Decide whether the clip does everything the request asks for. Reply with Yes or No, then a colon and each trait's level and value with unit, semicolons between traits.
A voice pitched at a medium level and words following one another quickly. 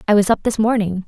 No: high, 210 Hz; fast, 280 wpm